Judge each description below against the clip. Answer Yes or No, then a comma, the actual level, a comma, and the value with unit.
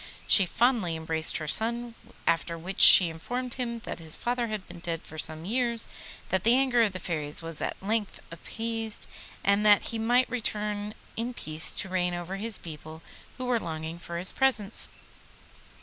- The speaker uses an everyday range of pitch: No, wide, 5.7 semitones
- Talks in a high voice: Yes, high, 200 Hz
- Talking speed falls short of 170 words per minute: No, average, 180 wpm